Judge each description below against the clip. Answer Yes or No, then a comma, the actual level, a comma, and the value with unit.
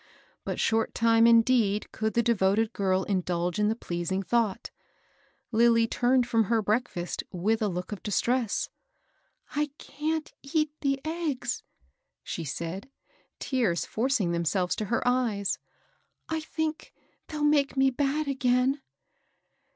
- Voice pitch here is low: No, high, 230 Hz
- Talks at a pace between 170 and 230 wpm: No, slow, 135 wpm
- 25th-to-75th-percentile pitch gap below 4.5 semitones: No, average, 5.2 semitones